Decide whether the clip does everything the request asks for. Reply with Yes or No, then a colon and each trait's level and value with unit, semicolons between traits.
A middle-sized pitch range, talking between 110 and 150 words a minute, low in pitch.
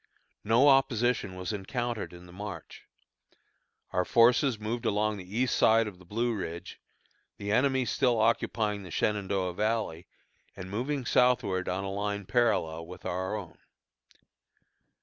Yes: average, 4.3 semitones; average, 140 wpm; low, 105 Hz